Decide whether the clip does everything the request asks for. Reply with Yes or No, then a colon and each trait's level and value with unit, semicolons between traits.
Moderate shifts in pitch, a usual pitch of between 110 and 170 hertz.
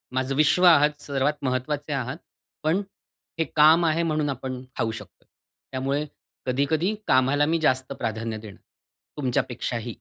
Yes: average, 3.1 semitones; medium, 140 Hz